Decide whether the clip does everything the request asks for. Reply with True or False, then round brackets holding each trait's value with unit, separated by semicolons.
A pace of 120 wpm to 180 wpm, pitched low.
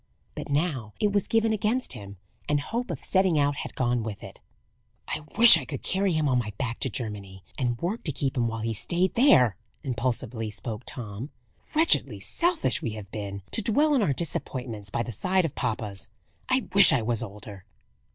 False (195 wpm; 125 Hz)